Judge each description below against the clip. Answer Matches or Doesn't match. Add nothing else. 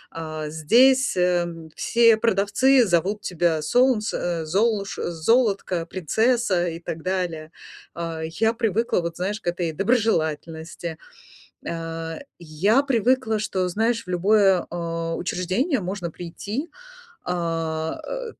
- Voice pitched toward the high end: Doesn't match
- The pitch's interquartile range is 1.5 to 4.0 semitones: Doesn't match